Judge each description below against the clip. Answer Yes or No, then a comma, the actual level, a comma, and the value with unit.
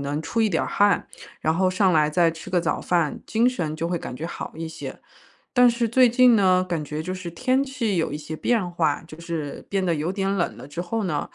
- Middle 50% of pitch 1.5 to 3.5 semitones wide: No, average, 4.7 semitones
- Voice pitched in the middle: Yes, medium, 175 Hz